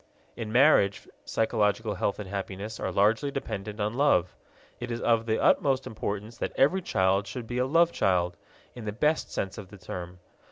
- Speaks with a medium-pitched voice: No, low, 110 Hz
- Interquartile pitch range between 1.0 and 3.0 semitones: No, average, 4.0 semitones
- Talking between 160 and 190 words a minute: Yes, average, 185 wpm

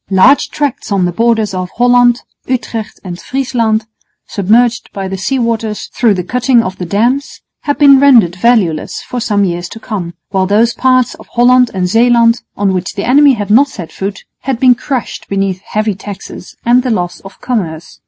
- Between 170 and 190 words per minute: Yes, average, 185 wpm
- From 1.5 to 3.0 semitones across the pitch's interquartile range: No, average, 4.4 semitones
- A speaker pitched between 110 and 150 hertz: No, high, 225 Hz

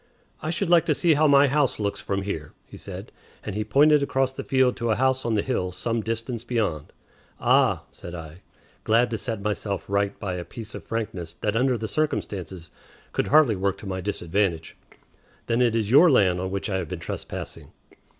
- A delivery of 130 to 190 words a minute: No, fast, 205 wpm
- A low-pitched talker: Yes, low, 110 Hz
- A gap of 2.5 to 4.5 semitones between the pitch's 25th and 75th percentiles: No, average, 5.3 semitones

